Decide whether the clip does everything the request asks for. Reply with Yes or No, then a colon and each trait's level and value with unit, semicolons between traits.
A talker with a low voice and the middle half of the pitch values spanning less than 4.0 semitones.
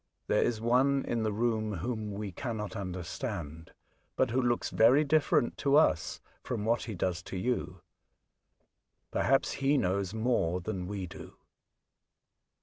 No: low, 110 Hz; average, 5.0 semitones